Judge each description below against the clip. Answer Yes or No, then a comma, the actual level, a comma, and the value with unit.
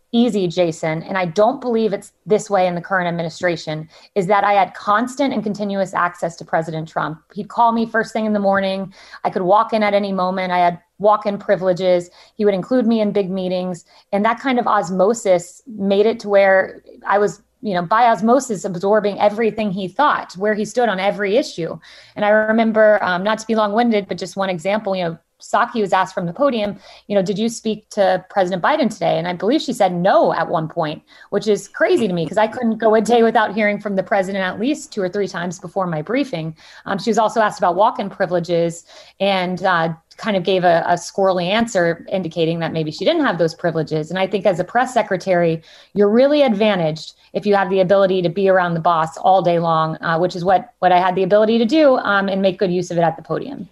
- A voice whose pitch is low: No, high, 195 Hz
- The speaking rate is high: Yes, fast, 235 wpm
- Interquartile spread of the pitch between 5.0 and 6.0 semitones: No, average, 3.3 semitones